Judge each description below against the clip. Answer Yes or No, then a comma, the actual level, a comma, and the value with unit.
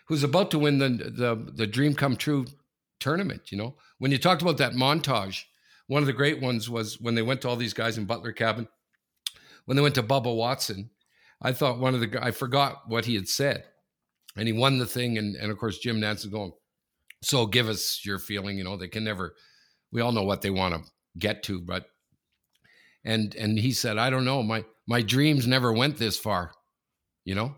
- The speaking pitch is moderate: No, low, 115 Hz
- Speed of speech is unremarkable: No, fast, 220 wpm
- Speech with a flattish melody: No, average, 3.9 semitones